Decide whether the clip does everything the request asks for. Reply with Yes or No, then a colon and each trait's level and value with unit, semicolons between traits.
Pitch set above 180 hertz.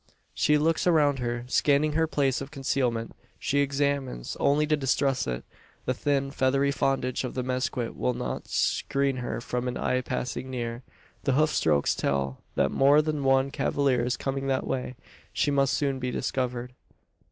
No: low, 135 Hz